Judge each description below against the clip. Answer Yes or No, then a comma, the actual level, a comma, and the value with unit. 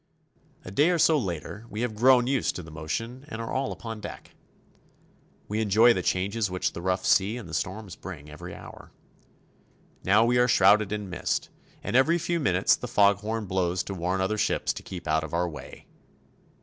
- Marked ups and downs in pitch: No, average, 4.2 semitones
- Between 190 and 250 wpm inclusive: Yes, average, 200 wpm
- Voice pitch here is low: Yes, low, 100 Hz